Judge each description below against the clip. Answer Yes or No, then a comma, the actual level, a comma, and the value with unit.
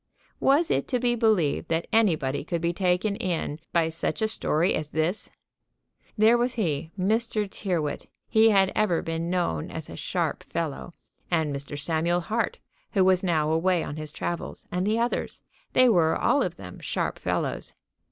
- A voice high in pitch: No, medium, 180 Hz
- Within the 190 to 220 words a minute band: No, average, 170 wpm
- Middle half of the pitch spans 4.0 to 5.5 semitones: Yes, average, 5.2 semitones